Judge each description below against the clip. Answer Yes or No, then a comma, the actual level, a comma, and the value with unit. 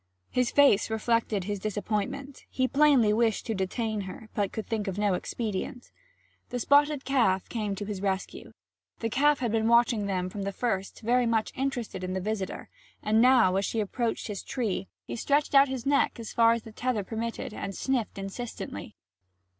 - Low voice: No, high, 225 Hz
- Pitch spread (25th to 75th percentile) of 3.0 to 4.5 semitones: Yes, average, 3.7 semitones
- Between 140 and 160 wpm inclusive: No, average, 185 wpm